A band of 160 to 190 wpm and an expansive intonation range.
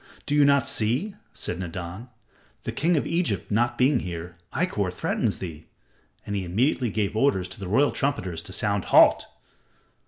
Yes: average, 165 wpm; wide, 7.3 semitones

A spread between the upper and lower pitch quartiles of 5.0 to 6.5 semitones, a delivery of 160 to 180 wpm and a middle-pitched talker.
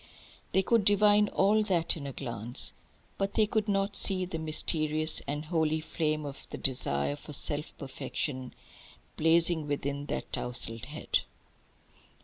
No: average, 5.3 semitones; average, 140 wpm; medium, 155 Hz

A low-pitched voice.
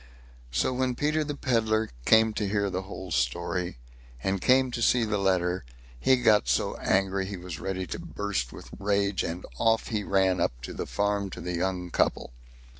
Yes: low, 100 Hz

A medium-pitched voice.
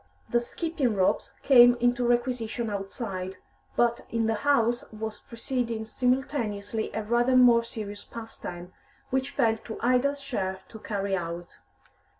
No: high, 230 Hz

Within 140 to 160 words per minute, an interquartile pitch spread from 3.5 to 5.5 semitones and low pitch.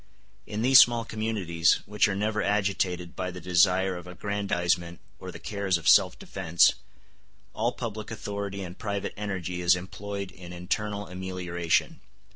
No: average, 145 wpm; narrow, 2.6 semitones; very low, 95 Hz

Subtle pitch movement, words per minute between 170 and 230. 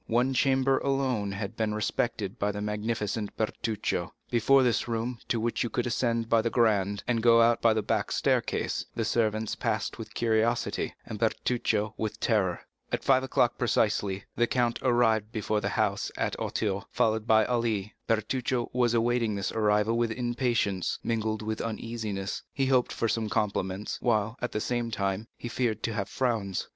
Yes: narrow, 2.1 semitones; average, 175 wpm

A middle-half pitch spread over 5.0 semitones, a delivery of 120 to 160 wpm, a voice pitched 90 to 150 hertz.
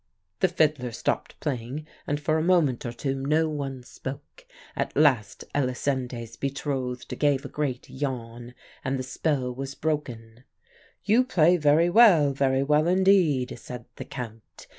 No: average, 3.6 semitones; average, 145 wpm; medium, 140 Hz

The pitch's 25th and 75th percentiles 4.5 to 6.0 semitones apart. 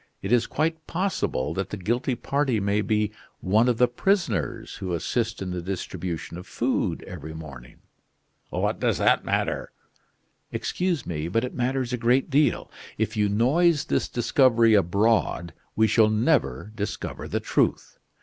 Yes: average, 5.2 semitones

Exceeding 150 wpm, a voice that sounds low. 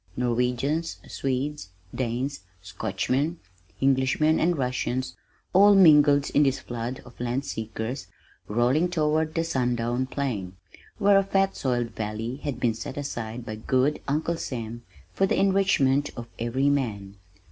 No: slow, 135 wpm; low, 130 Hz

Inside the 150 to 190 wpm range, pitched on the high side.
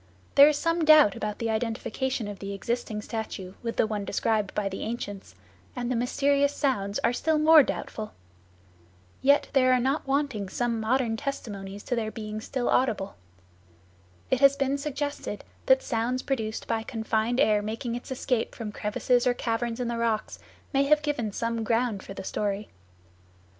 Yes: average, 170 wpm; high, 235 Hz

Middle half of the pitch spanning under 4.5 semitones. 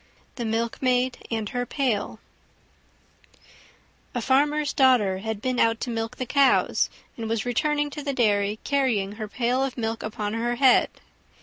Yes: average, 2.9 semitones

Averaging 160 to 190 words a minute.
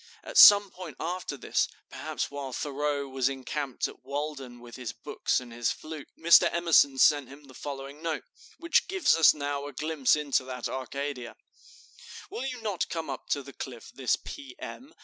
Yes: average, 180 wpm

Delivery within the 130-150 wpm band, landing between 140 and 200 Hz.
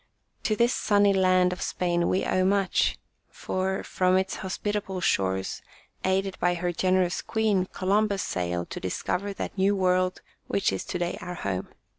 No: average, 160 wpm; medium, 185 Hz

